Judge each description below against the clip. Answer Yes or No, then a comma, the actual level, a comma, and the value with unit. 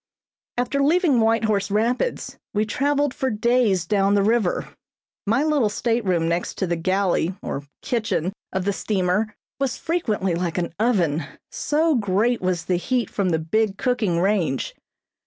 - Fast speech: No, average, 150 wpm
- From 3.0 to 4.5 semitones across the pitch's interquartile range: No, average, 5.1 semitones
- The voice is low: No, high, 210 Hz